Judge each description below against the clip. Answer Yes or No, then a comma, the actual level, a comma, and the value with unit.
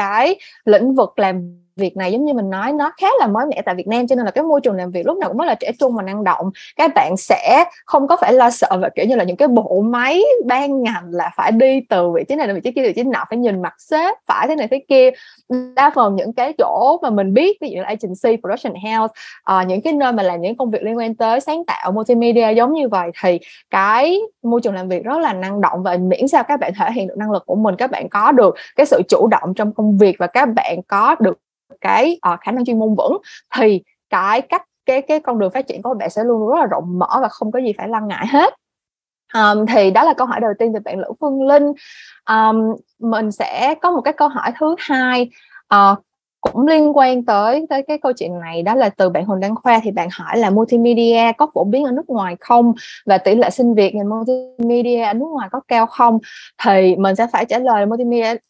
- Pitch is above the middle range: Yes, high, 235 Hz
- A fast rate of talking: Yes, fast, 255 wpm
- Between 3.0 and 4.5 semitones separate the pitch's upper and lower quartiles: No, average, 5.2 semitones